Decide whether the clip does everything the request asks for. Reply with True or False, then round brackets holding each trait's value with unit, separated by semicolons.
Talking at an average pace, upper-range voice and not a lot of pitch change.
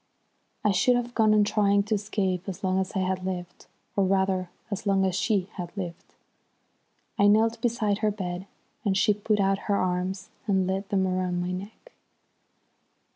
True (180 wpm; 195 Hz; 2.1 semitones)